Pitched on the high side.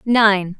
Yes: high, 205 Hz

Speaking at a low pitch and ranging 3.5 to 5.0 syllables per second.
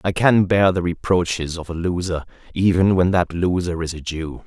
Yes: very low, 90 Hz; 4.9 syllables/s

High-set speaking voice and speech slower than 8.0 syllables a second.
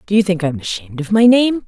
Yes: high, 195 Hz; 7.2 syllables/s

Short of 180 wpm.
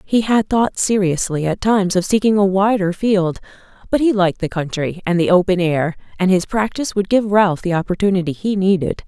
No: average, 200 wpm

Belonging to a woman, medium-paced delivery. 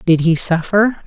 Yes: female; average, 170 wpm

